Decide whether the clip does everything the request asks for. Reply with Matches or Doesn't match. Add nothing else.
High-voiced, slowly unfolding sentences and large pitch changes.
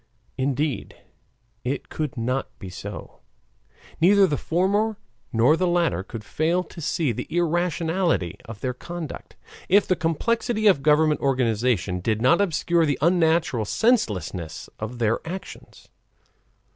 Doesn't match